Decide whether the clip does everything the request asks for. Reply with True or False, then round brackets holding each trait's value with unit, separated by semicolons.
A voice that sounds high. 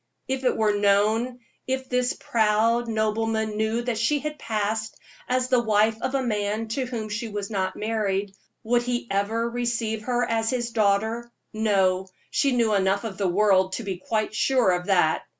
True (220 Hz)